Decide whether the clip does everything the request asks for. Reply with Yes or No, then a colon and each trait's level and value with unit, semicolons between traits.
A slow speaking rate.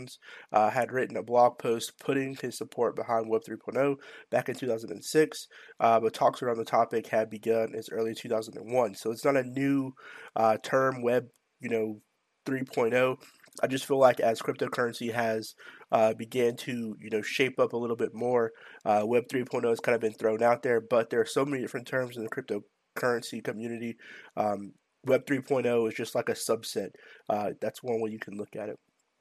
No: average, 195 wpm